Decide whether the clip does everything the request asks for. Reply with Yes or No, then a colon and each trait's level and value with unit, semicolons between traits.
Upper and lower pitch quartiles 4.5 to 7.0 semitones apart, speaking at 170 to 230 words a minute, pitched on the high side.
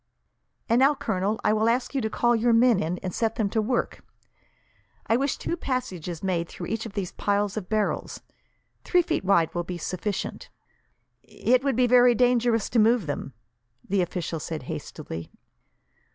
Yes: average, 4.9 semitones; average, 175 wpm; high, 220 Hz